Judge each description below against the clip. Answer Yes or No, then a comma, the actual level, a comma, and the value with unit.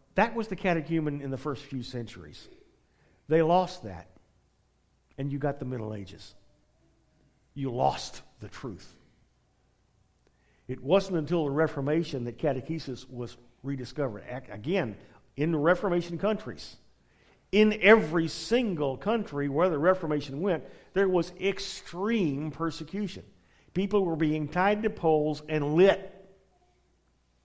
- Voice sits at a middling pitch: Yes, medium, 155 Hz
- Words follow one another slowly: Yes, slow, 120 wpm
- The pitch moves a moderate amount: No, wide, 6.4 semitones